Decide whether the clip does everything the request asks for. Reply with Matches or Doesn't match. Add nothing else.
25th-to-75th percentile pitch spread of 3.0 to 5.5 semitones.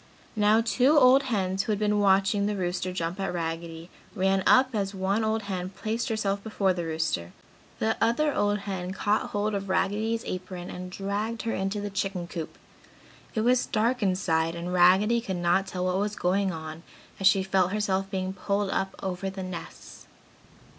Doesn't match